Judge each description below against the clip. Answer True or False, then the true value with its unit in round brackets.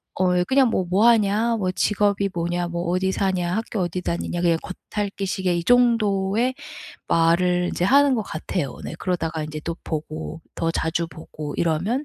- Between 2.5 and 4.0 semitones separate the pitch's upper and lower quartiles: True (3.5 semitones)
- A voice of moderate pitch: True (180 Hz)